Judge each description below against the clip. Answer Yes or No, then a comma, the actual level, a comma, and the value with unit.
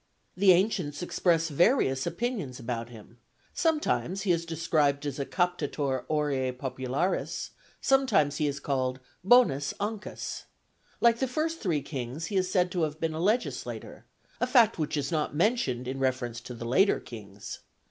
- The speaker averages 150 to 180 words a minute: Yes, average, 155 wpm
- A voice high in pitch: No, medium, 155 Hz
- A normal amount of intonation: No, wide, 6.4 semitones